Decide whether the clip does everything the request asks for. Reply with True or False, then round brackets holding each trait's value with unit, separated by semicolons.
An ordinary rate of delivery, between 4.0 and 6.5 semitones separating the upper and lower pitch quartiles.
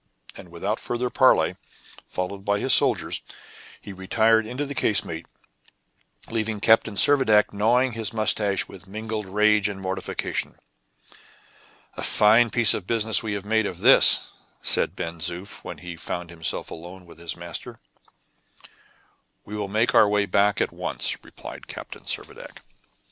False (145 wpm; 3.0 semitones)